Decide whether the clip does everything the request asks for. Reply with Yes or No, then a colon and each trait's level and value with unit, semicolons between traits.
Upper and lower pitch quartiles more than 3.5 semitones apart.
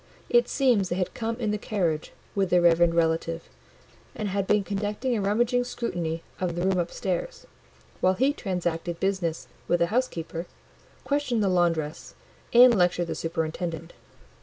Yes: average, 4.5 semitones